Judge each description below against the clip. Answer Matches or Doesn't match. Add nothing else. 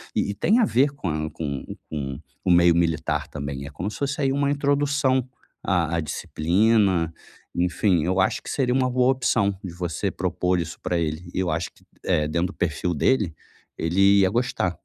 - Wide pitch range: Matches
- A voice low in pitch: Matches